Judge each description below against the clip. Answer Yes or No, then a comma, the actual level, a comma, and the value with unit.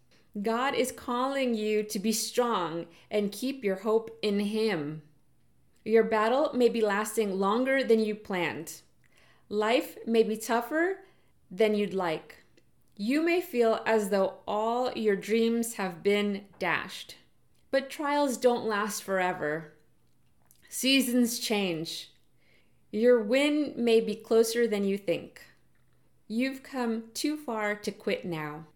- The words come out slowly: Yes, slow, 130 wpm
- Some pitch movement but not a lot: Yes, average, 3.7 semitones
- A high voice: Yes, high, 220 Hz